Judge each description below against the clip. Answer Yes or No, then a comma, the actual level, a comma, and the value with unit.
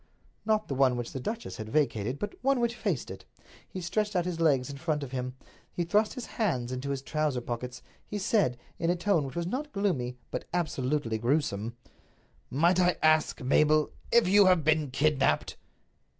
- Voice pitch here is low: No, medium, 155 Hz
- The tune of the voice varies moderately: No, wide, 6.5 semitones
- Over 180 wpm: Yes, average, 190 wpm